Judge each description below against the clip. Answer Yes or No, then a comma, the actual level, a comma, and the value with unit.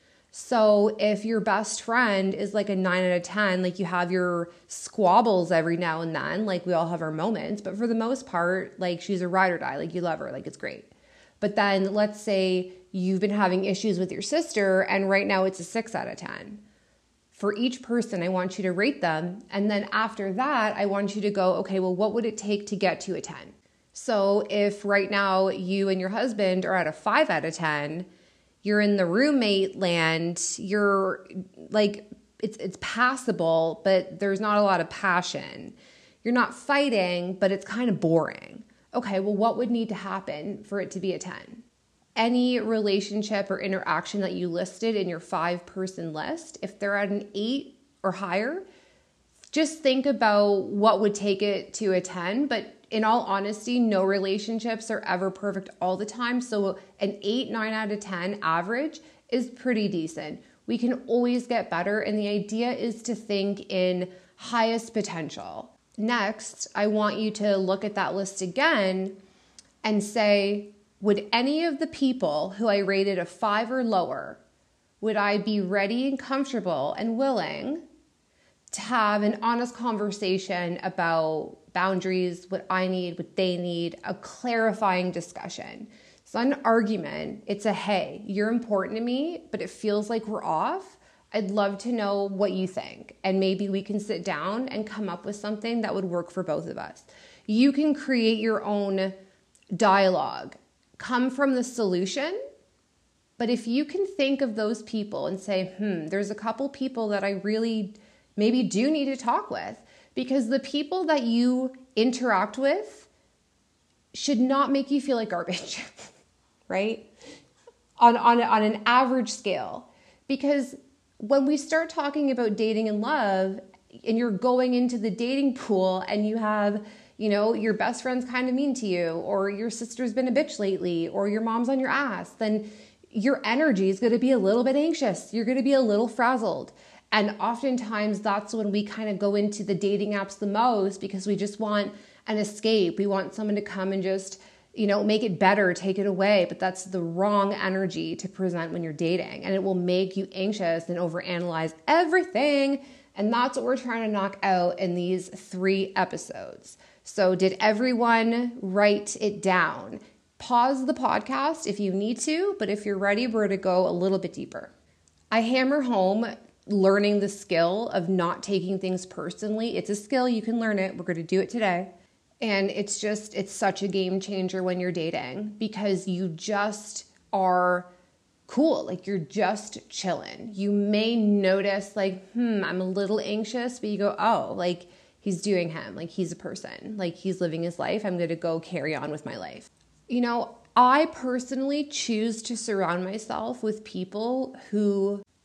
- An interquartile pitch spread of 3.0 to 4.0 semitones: Yes, average, 3.5 semitones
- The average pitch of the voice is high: Yes, high, 205 Hz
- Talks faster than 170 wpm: Yes, average, 185 wpm